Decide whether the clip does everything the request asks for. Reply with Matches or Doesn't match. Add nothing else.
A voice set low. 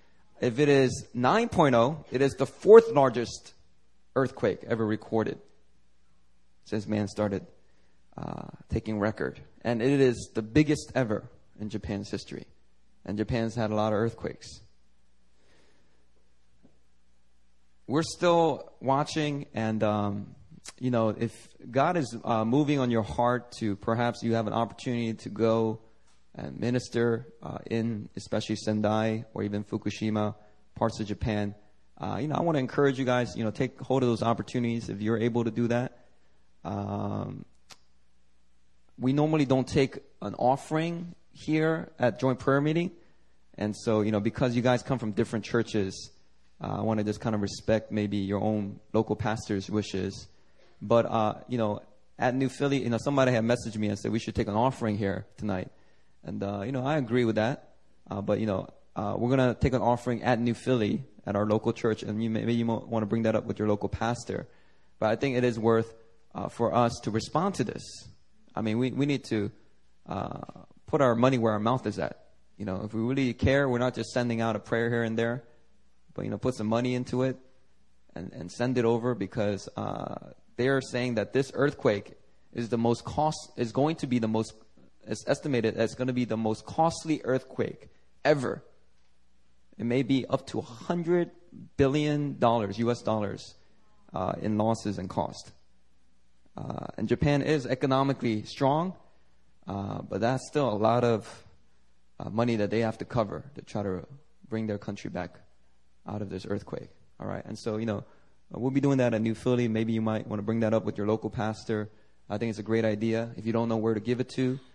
Matches